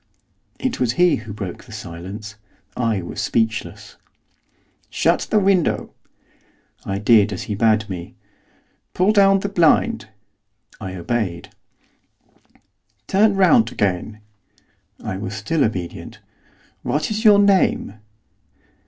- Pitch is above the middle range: No, low, 110 Hz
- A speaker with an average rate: No, slow, 115 wpm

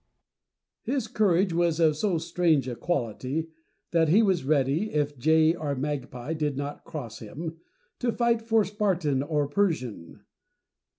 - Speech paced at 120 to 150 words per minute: Yes, average, 140 wpm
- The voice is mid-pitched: Yes, medium, 160 Hz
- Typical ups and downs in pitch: Yes, average, 4.3 semitones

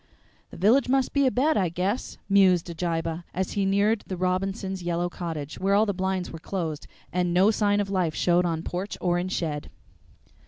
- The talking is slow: No, average, 190 wpm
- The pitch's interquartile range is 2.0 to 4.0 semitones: Yes, narrow, 2.6 semitones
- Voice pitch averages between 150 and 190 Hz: Yes, medium, 185 Hz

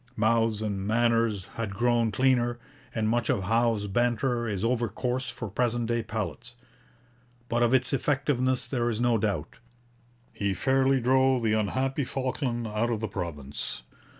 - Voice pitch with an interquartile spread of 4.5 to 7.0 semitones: No, average, 2.7 semitones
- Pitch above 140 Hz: No, low, 115 Hz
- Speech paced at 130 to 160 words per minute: Yes, average, 150 wpm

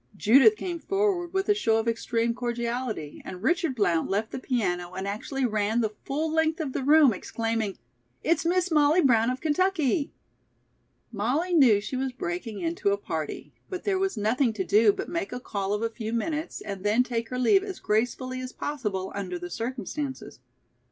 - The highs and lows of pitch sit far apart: Yes, wide, 6.7 semitones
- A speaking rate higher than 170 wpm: Yes, average, 185 wpm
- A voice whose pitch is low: No, very high, 250 Hz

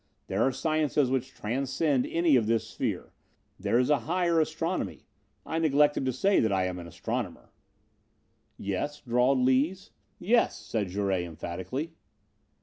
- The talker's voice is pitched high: No, low, 135 Hz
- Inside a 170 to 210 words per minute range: No, average, 145 wpm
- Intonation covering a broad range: Yes, wide, 6.3 semitones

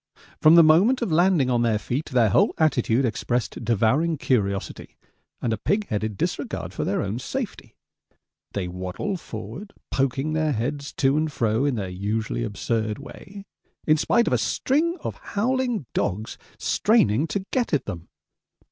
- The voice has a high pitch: No, low, 135 Hz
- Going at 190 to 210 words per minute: No, average, 160 wpm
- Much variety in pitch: Yes, wide, 7.6 semitones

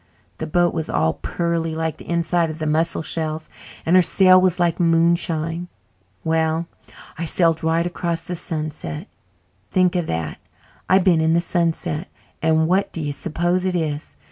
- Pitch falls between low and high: Yes, medium, 165 Hz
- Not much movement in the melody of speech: Yes, narrow, 1.6 semitones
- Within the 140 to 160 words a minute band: No, average, 170 wpm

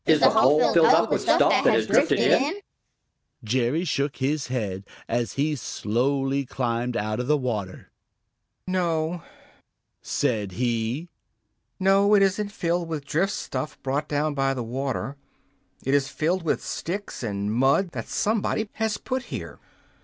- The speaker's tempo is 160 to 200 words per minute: No, average, 150 wpm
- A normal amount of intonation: No, wide, 5.8 semitones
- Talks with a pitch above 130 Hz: Yes, medium, 140 Hz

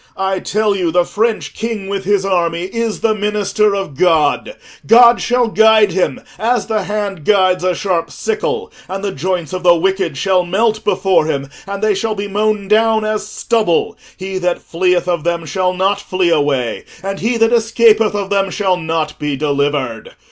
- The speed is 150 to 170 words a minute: No, average, 185 wpm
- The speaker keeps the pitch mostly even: No, average, 3.5 semitones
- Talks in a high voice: Yes, high, 195 Hz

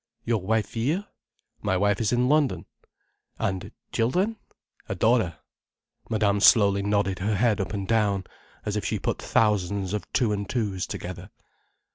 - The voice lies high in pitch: No, low, 105 Hz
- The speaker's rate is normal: Yes, average, 150 wpm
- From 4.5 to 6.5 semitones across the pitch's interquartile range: No, average, 2.7 semitones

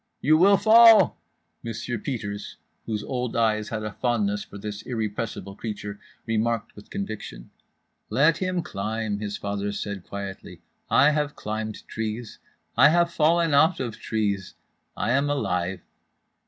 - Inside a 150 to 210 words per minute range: No, slow, 135 wpm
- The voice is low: Yes, low, 110 Hz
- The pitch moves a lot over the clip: Yes, wide, 5.8 semitones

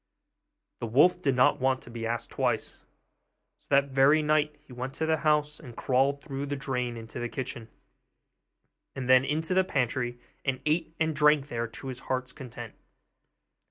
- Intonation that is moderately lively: Yes, average, 3.2 semitones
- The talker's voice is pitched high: No, low, 135 Hz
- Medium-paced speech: Yes, average, 175 wpm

